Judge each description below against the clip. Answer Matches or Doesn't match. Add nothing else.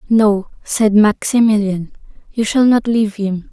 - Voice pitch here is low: Doesn't match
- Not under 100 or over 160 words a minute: Matches